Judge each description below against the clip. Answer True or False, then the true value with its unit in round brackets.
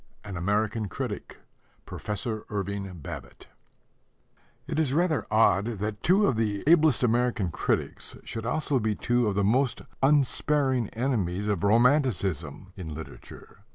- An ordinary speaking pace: False (130 wpm)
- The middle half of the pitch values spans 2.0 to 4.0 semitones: False (4.7 semitones)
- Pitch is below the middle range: True (110 Hz)